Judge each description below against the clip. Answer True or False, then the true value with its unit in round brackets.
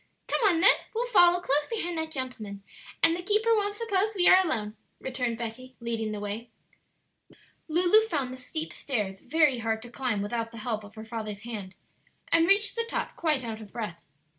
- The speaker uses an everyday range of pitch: False (8.0 semitones)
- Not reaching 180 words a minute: False (190 wpm)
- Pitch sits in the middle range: False (255 Hz)